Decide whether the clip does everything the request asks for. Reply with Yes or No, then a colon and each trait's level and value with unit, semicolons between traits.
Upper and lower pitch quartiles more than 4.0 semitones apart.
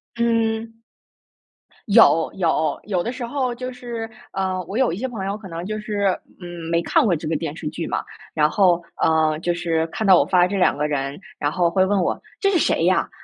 Yes: average, 5.3 semitones